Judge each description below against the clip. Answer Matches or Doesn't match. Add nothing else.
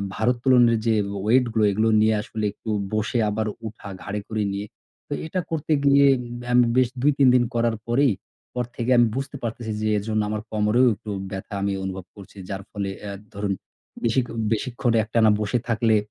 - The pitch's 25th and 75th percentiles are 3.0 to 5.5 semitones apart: Doesn't match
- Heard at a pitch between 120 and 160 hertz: Doesn't match